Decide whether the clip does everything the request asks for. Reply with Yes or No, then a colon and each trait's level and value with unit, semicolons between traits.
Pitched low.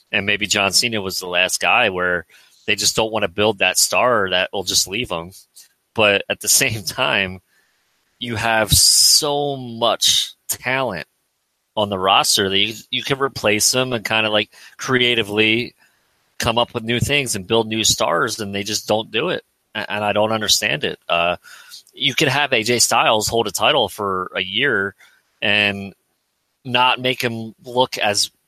Yes: low, 110 Hz